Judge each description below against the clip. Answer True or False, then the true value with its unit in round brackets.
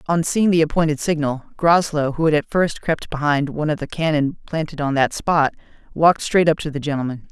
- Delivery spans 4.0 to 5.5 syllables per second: False (5.7 syllables/s)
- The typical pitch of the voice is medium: True (155 Hz)